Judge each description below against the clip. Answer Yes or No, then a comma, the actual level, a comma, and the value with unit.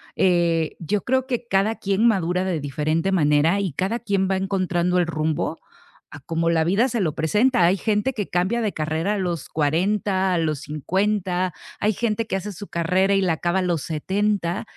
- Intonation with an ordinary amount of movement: Yes, average, 3.7 semitones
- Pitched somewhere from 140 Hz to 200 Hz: Yes, medium, 185 Hz